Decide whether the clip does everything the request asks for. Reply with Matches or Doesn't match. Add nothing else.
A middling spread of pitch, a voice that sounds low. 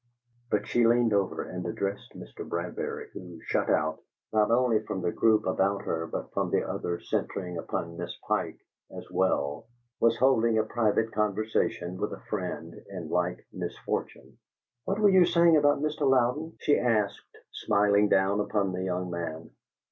Matches